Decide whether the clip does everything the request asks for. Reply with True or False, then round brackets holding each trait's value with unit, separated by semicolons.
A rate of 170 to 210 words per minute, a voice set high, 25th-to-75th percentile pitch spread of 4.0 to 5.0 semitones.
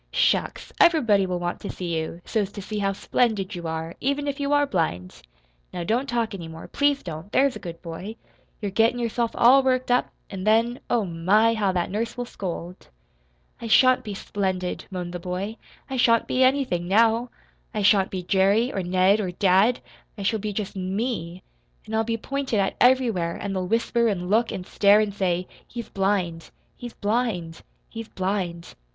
True (190 wpm; 205 Hz; 4.4 semitones)